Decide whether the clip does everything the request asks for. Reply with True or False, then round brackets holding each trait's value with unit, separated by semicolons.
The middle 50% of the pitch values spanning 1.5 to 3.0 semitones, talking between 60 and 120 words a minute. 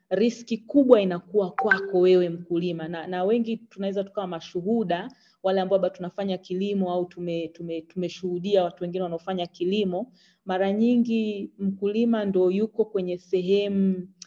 False (2.6 semitones; 135 wpm)